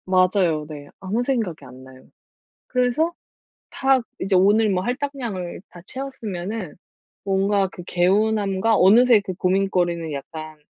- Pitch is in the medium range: No, high, 195 Hz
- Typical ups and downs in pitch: Yes, average, 4.4 semitones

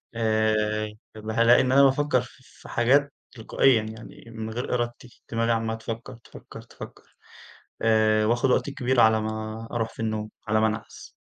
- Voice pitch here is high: No, low, 115 Hz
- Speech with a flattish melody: Yes, narrow, 1.8 semitones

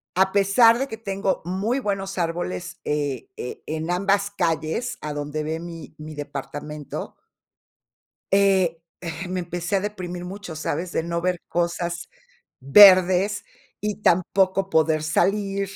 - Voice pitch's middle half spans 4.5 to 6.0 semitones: No, average, 3.6 semitones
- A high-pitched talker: No, medium, 180 Hz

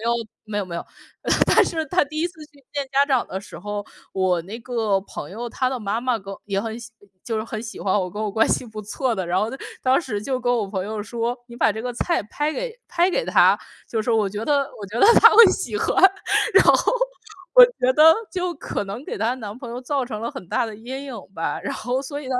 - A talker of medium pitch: No, high, 235 Hz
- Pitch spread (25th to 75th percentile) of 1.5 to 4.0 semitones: No, average, 4.7 semitones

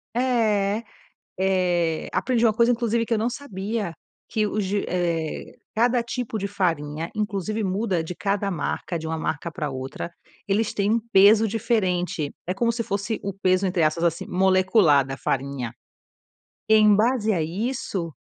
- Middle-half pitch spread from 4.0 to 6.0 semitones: Yes, average, 4.4 semitones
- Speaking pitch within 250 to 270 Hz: No, high, 195 Hz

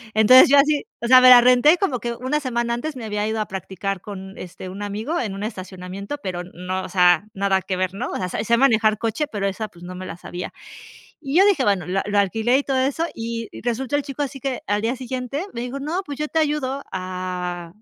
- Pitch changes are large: Yes, wide, 5.7 semitones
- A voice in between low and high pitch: No, high, 225 Hz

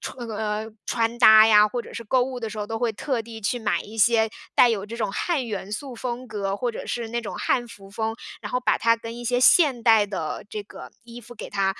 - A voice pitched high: Yes, high, 225 Hz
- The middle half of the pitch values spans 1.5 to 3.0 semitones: Yes, narrow, 2.4 semitones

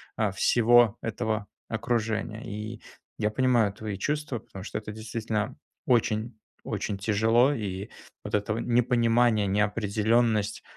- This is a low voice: Yes, low, 110 Hz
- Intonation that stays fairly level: Yes, narrow, 1.9 semitones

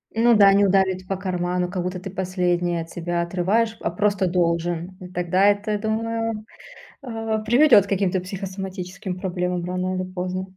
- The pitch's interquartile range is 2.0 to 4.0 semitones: Yes, narrow, 2.4 semitones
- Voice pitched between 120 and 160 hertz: No, medium, 185 Hz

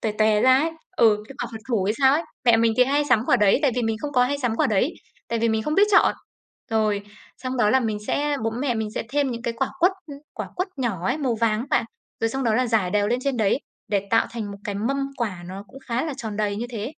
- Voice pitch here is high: Yes, high, 230 Hz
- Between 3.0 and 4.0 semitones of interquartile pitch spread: Yes, average, 3.7 semitones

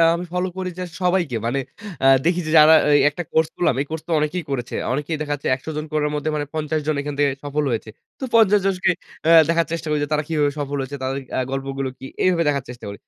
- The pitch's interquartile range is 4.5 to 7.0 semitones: No, average, 3.2 semitones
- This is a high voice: No, medium, 150 Hz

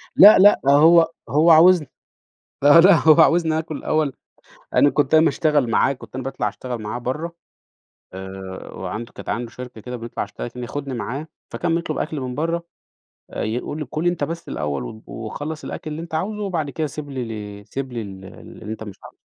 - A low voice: No, medium, 145 Hz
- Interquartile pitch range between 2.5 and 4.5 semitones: No, average, 5.2 semitones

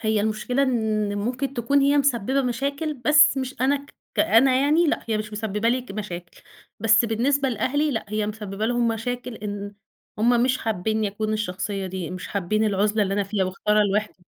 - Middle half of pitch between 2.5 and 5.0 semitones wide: Yes, average, 3.8 semitones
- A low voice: No, high, 220 Hz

